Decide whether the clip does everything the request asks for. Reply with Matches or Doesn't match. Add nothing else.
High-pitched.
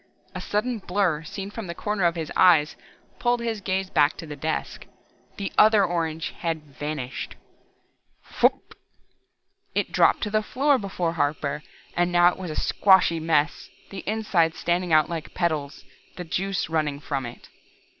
Doesn't match